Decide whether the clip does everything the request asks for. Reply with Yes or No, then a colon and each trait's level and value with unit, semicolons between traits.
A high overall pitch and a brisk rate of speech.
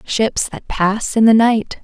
No: high, 220 Hz; average, 195 wpm